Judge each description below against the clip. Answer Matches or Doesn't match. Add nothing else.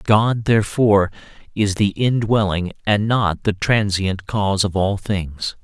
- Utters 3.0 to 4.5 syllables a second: Matches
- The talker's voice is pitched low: Matches